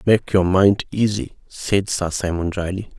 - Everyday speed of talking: Yes, average, 160 wpm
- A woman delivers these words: No, male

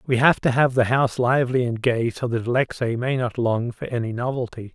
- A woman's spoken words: No, male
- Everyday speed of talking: No, fast, 230 wpm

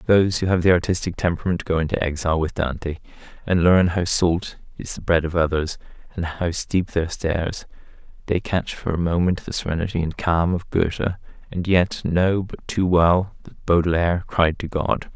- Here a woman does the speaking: No, male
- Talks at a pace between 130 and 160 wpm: No, average, 185 wpm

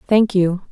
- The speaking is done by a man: No, female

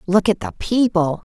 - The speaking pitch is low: No, medium, 185 Hz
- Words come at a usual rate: Yes, average, 185 wpm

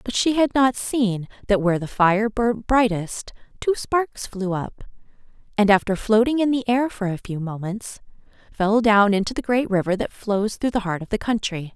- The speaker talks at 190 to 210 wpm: Yes, average, 200 wpm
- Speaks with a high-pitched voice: Yes, high, 215 Hz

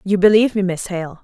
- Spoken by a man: No, female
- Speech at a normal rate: No, fast, 245 wpm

